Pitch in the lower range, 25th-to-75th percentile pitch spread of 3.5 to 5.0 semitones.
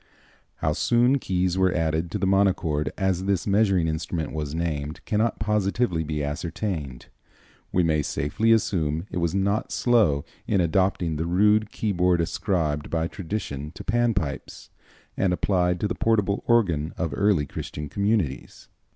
Yes: very low, 90 Hz; average, 4.5 semitones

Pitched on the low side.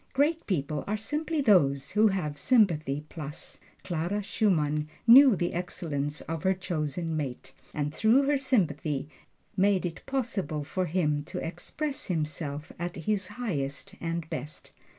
No: medium, 175 Hz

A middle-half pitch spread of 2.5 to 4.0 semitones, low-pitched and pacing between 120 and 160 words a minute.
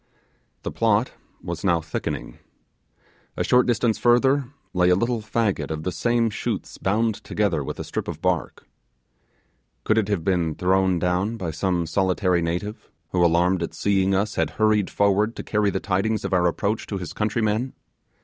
No: average, 3.5 semitones; low, 100 Hz; average, 170 wpm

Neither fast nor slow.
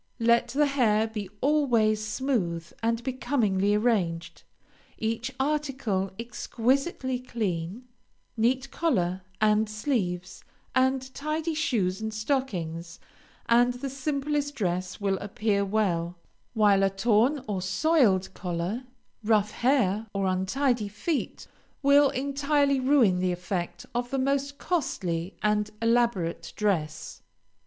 No: slow, 115 wpm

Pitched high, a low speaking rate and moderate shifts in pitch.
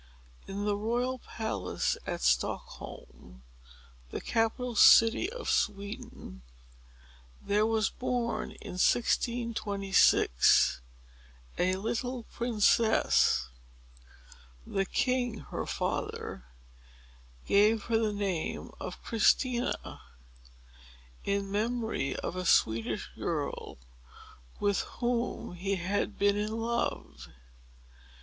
Yes: high, 215 Hz; slow, 90 wpm; average, 3.3 semitones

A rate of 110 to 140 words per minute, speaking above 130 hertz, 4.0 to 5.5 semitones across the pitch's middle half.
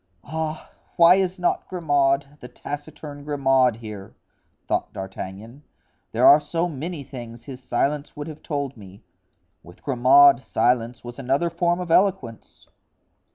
Yes: slow, 135 wpm; medium, 140 Hz; average, 4.5 semitones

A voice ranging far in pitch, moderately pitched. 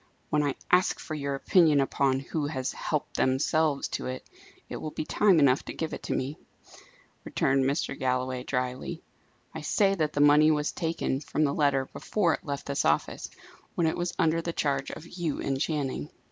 No: average, 3.0 semitones; medium, 145 Hz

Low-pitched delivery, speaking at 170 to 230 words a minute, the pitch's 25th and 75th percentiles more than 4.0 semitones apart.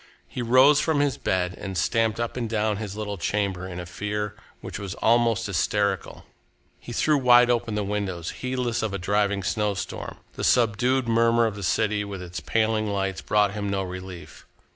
No: low, 105 Hz; average, 185 wpm; average, 3.0 semitones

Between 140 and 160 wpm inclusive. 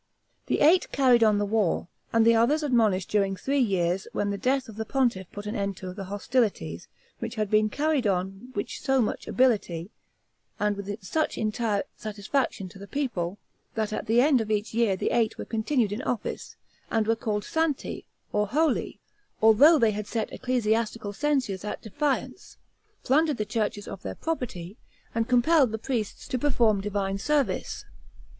No: average, 175 wpm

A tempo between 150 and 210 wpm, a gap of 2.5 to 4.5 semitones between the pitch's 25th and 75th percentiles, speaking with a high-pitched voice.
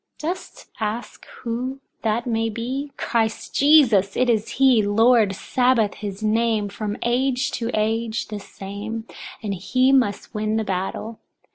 No: average, 140 wpm; average, 2.8 semitones; high, 225 Hz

